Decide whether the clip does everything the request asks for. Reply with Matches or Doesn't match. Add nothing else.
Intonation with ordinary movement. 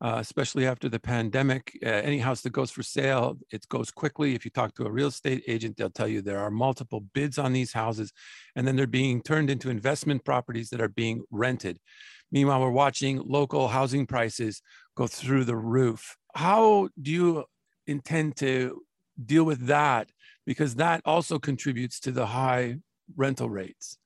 Matches